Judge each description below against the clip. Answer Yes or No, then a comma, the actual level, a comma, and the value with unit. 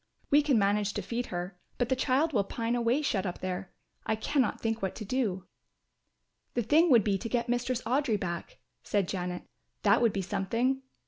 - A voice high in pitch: Yes, high, 230 Hz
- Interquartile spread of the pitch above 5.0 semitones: No, average, 4.6 semitones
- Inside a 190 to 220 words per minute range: Yes, average, 195 wpm